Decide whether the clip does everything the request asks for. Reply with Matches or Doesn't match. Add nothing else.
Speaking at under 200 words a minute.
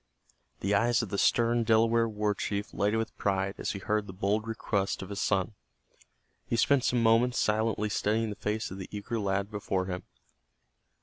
Matches